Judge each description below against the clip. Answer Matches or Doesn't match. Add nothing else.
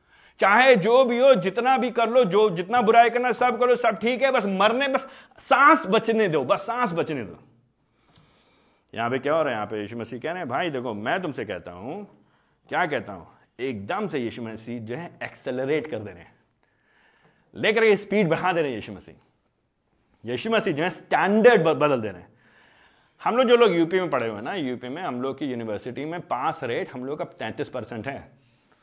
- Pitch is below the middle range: Doesn't match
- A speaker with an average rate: Doesn't match